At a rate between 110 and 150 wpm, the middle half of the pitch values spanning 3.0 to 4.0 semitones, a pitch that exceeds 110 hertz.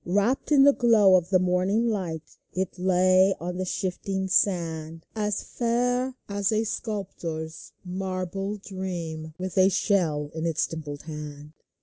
Yes: average, 140 wpm; average, 3.6 semitones; medium, 185 Hz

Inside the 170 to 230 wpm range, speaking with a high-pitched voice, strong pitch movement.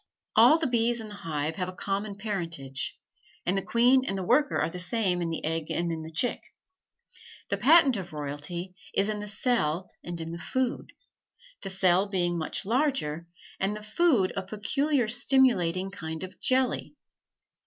Yes: average, 175 wpm; high, 195 Hz; wide, 5.8 semitones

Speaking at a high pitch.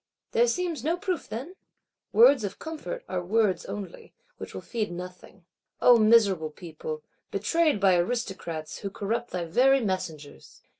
Yes: high, 215 Hz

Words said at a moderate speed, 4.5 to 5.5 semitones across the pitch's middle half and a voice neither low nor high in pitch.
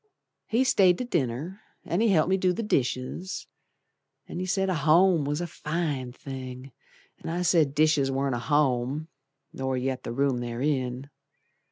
Yes: average, 170 wpm; average, 5.2 semitones; medium, 150 Hz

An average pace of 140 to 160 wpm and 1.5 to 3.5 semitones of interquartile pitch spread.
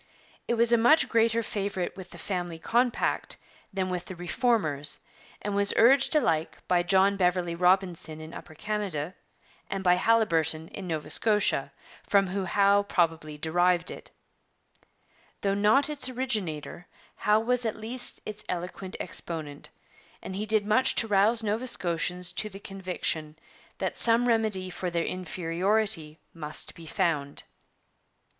No: average, 145 wpm; average, 4.3 semitones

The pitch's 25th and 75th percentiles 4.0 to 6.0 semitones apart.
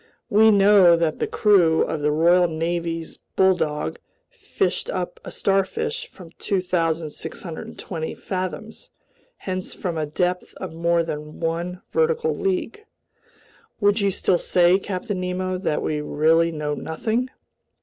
No: average, 3.3 semitones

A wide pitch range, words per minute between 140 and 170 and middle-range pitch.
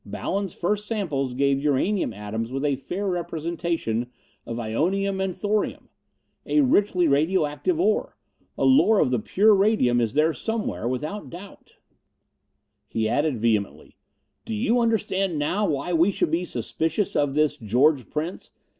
Yes: wide, 6.8 semitones; average, 145 wpm; medium, 165 Hz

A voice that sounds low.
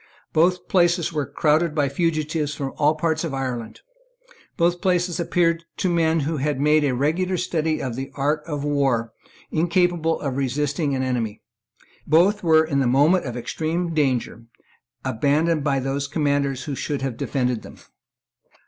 No: medium, 150 Hz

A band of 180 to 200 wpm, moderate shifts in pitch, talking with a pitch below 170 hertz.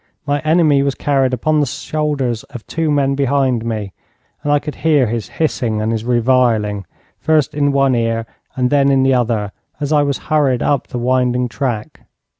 Yes: average, 185 wpm; average, 3.5 semitones; low, 135 Hz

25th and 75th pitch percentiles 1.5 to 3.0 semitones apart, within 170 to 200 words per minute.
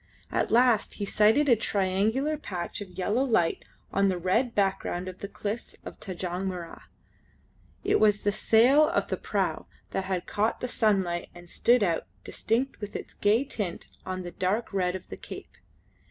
No: average, 3.6 semitones; average, 175 wpm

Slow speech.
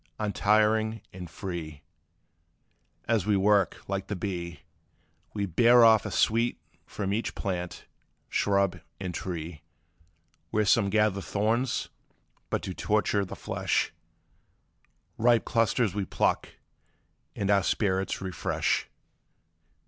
Yes: slow, 110 wpm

